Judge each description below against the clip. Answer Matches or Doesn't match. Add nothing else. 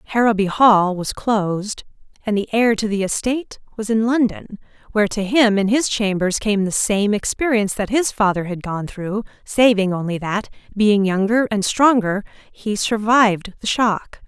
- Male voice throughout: Doesn't match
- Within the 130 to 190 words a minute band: Matches